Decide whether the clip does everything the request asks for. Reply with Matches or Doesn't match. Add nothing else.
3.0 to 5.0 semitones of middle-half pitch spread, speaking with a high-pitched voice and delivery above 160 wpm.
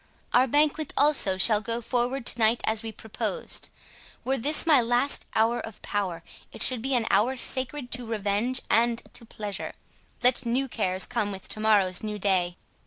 Matches